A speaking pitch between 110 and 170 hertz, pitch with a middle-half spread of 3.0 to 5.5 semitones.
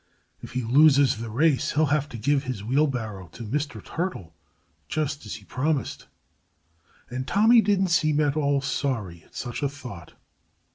Yes: medium, 140 Hz; average, 4.0 semitones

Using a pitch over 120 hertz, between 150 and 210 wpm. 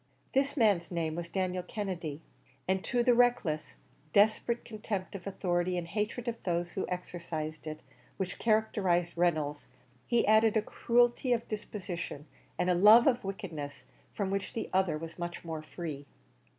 Yes: medium, 185 Hz; average, 155 wpm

